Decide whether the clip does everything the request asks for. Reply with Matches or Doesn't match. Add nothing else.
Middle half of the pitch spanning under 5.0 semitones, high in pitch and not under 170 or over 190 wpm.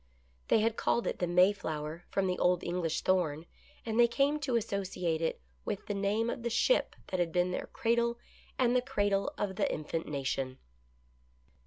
Doesn't match